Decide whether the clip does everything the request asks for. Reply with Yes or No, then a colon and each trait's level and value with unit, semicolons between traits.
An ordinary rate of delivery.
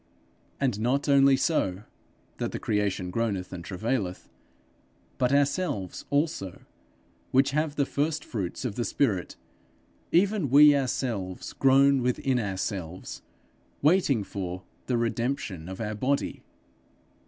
No: slow, 120 wpm